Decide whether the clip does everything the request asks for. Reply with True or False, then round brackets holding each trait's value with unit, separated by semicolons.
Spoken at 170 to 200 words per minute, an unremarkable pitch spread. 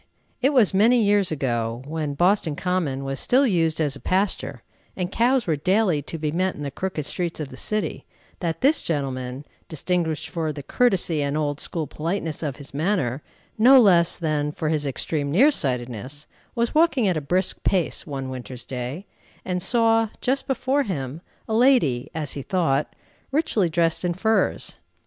False (175 wpm; 6.2 semitones)